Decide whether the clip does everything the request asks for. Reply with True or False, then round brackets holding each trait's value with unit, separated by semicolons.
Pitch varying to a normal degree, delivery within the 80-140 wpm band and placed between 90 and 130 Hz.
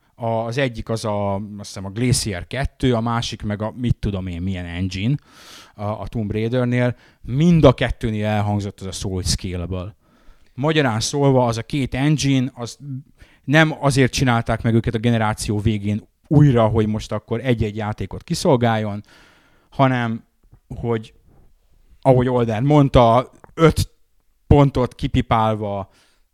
True (3.6 semitones; 135 wpm; 115 Hz)